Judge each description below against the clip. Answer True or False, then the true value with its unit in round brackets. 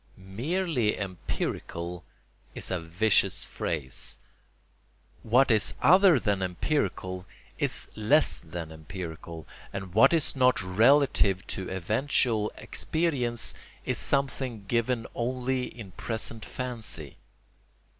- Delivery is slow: True (100 wpm)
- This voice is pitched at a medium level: False (110 Hz)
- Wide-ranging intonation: True (5.7 semitones)